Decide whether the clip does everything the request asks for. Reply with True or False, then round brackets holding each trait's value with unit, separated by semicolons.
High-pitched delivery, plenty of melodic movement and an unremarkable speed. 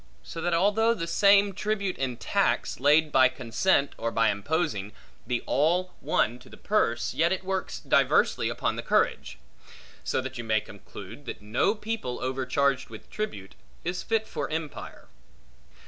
False (145 Hz; 8.0 semitones; 160 wpm)